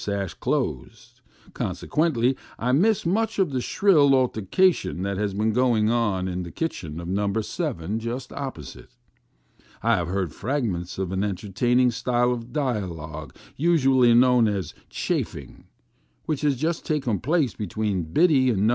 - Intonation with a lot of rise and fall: Yes, wide, 6.0 semitones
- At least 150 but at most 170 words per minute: Yes, average, 155 wpm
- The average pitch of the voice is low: Yes, low, 115 Hz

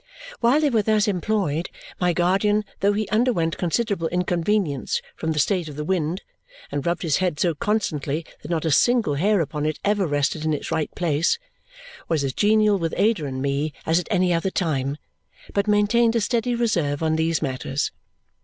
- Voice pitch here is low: No, medium, 175 Hz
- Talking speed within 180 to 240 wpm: Yes, average, 185 wpm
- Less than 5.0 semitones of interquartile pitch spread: No, average, 5.3 semitones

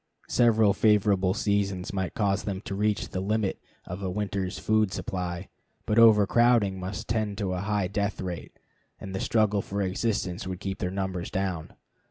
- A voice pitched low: Yes, low, 100 Hz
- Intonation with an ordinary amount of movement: No, narrow, 2.1 semitones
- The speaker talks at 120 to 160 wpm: No, average, 170 wpm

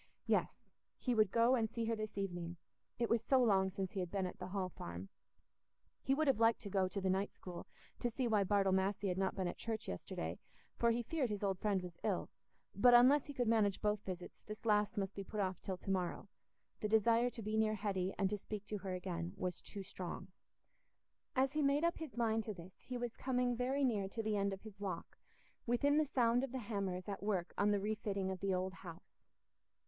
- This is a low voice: No, high, 205 Hz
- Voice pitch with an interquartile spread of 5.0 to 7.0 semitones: No, average, 3.5 semitones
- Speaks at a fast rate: Yes, fast, 225 wpm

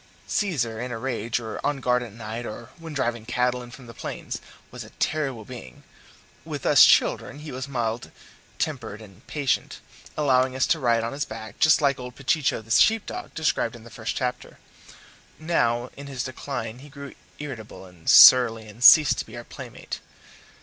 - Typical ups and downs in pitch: Yes, average, 3.5 semitones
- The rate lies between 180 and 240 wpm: Yes, average, 185 wpm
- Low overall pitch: Yes, low, 125 Hz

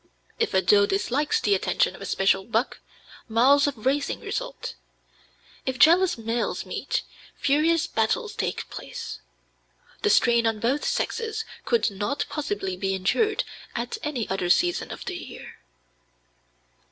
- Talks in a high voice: Yes, very high, 255 Hz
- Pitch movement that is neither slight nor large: No, wide, 8.2 semitones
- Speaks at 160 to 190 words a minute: No, average, 140 wpm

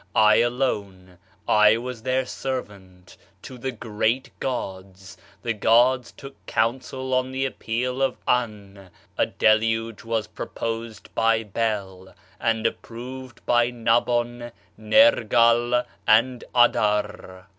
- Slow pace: Yes, slow, 110 wpm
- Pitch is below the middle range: Yes, low, 115 Hz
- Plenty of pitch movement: No, average, 2.7 semitones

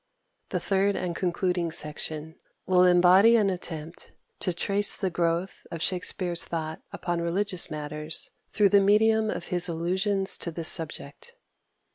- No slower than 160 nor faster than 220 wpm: No, average, 140 wpm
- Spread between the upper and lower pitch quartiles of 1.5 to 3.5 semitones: Yes, average, 2.8 semitones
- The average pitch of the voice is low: No, medium, 180 Hz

